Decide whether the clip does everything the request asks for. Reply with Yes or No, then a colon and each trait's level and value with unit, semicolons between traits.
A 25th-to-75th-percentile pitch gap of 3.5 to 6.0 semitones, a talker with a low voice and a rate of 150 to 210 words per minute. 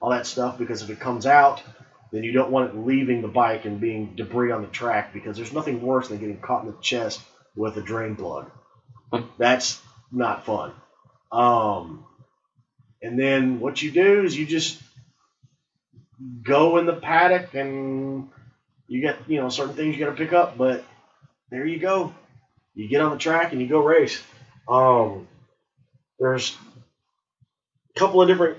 Yes: average, 4.0 semitones; low, 130 Hz; average, 175 wpm